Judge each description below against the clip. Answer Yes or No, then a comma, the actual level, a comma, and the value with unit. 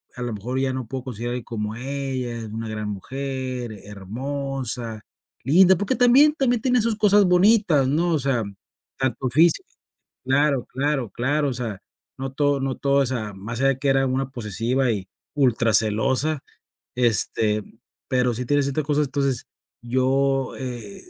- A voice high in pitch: No, low, 130 Hz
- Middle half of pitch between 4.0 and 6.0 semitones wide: No, average, 3.3 semitones